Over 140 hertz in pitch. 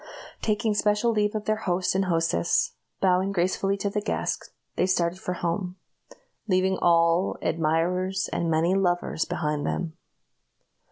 Yes: medium, 185 Hz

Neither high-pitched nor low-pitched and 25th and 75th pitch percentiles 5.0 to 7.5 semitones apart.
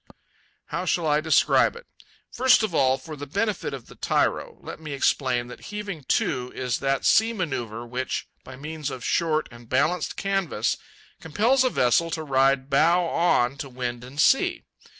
Yes: medium, 150 Hz; wide, 5.4 semitones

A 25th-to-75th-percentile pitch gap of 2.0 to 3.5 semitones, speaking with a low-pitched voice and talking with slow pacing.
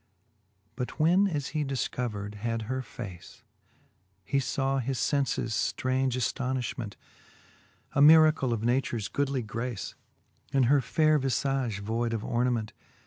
Yes: average, 3.2 semitones; low, 130 Hz; slow, 125 wpm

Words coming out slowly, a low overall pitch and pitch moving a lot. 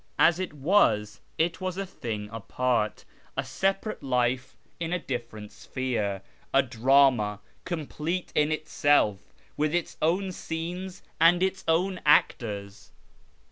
No: slow, 125 wpm; medium, 145 Hz; wide, 7.1 semitones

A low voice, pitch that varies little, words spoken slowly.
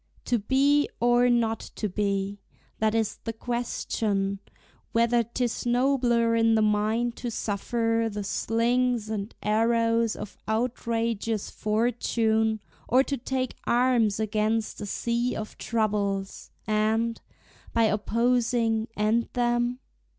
No: high, 230 Hz; narrow, 2.0 semitones; slow, 120 wpm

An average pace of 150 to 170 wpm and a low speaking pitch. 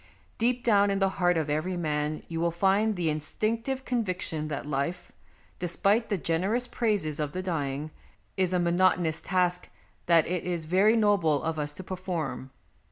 No: average, 165 wpm; medium, 180 Hz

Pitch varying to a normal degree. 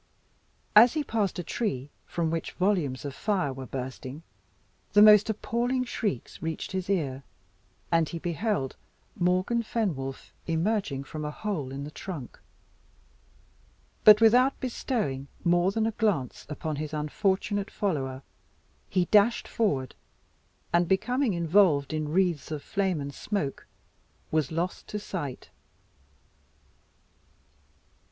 No: wide, 6.3 semitones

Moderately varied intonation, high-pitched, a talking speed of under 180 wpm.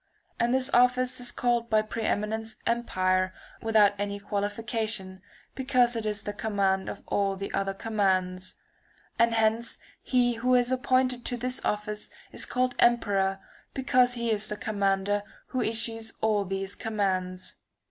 Yes: average, 3.2 semitones; high, 220 Hz; average, 150 wpm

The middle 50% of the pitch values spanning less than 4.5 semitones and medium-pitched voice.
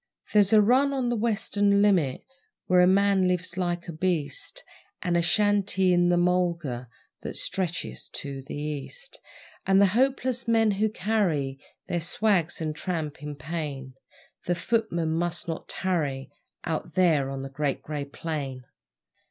No: average, 5.1 semitones; medium, 175 Hz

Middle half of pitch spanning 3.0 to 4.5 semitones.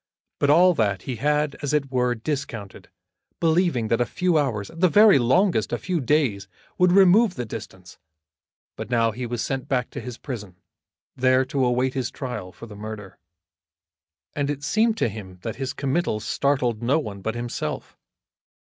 No: average, 5.0 semitones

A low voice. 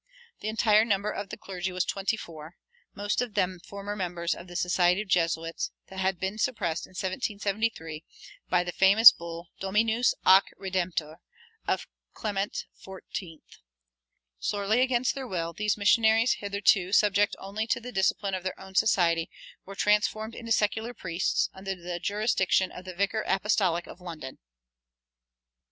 No: high, 195 Hz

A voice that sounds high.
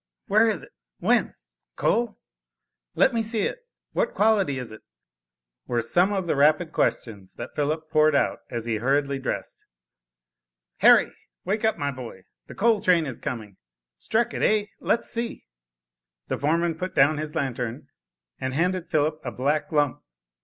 No: medium, 155 Hz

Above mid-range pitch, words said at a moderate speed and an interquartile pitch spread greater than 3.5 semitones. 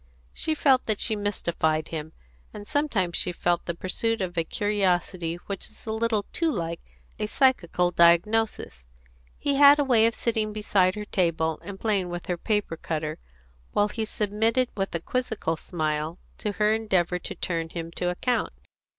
Yes: high, 195 Hz; average, 170 wpm; average, 4.5 semitones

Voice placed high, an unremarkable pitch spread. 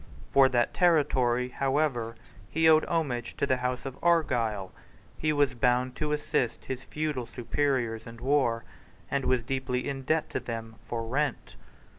No: low, 130 Hz; average, 3.4 semitones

